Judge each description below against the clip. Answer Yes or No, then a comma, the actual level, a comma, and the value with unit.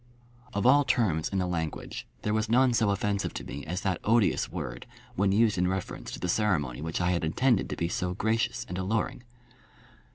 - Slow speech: No, average, 200 wpm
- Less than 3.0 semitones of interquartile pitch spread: No, average, 3.9 semitones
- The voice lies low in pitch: Yes, very low, 95 Hz